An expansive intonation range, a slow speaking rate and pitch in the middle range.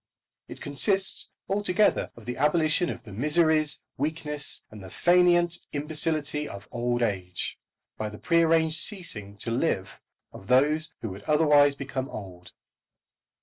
Yes: wide, 6.0 semitones; slow, 130 wpm; medium, 150 Hz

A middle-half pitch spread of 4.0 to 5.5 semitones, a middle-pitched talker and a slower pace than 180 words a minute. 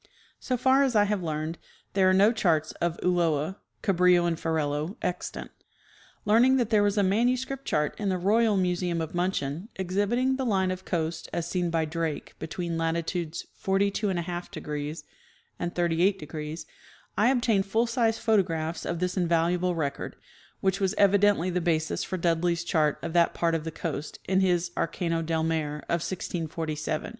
No: average, 3.4 semitones; medium, 175 Hz; average, 170 wpm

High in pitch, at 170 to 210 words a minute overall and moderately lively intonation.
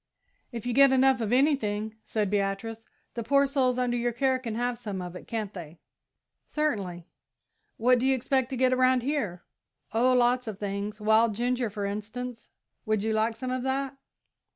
Yes: high, 235 Hz; average, 180 wpm; average, 3.3 semitones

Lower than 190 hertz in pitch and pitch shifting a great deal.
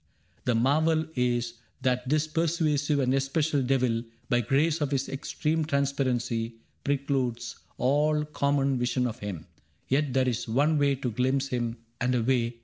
No: low, 135 Hz; average, 3.1 semitones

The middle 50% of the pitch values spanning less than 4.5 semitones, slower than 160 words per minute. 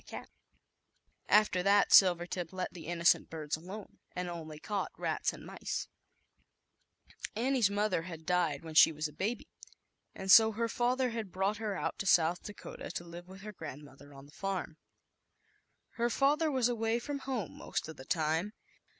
No: average, 5.3 semitones; average, 150 wpm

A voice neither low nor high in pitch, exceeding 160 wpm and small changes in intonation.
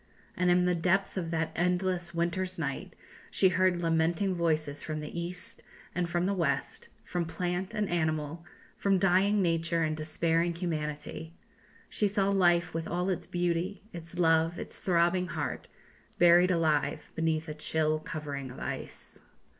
No: medium, 170 Hz; average, 155 wpm; narrow, 2.1 semitones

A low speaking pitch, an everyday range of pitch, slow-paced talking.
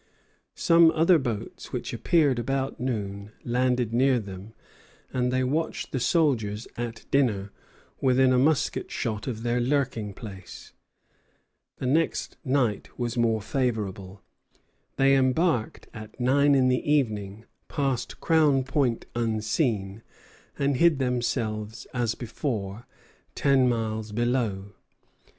Yes: low, 125 Hz; average, 3.8 semitones; slow, 120 wpm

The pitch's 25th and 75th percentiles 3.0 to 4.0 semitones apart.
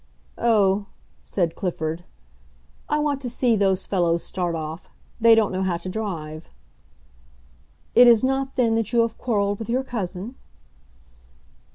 No: average, 4.9 semitones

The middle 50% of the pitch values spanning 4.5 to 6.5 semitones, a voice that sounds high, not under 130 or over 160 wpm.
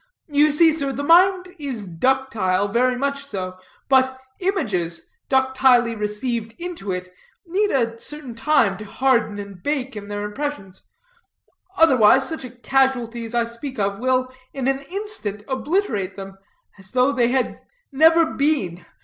Yes: wide, 5.4 semitones; very high, 255 Hz; average, 150 wpm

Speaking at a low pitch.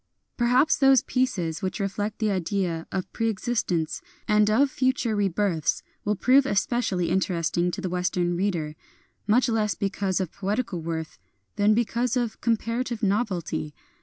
No: high, 205 Hz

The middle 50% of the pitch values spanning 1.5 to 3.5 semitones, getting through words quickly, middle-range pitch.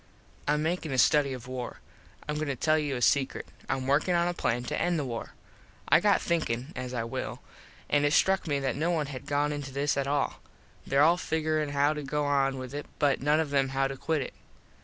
Yes: narrow, 2.4 semitones; fast, 235 wpm; medium, 145 Hz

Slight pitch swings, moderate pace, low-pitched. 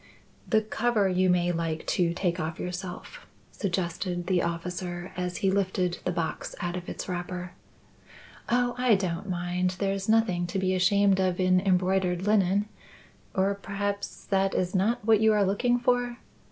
No: narrow, 2.2 semitones; average, 160 wpm; medium, 185 Hz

